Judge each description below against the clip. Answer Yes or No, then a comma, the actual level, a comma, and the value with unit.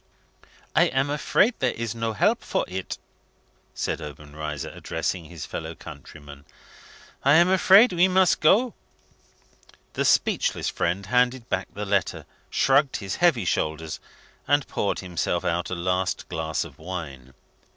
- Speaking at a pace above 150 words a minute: No, average, 140 wpm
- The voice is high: No, low, 100 Hz